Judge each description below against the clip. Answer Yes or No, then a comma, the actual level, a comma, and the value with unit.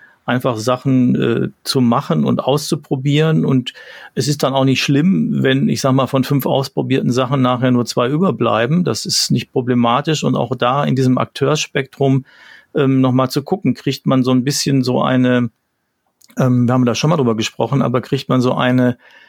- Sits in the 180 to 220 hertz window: No, low, 130 Hz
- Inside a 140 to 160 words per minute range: No, fast, 190 wpm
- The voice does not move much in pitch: Yes, narrow, 2.1 semitones